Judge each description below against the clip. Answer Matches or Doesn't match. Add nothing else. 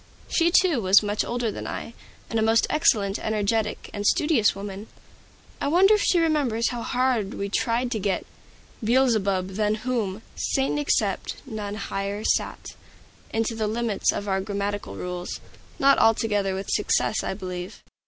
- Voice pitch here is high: Matches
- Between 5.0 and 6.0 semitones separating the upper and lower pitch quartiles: Doesn't match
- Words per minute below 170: Matches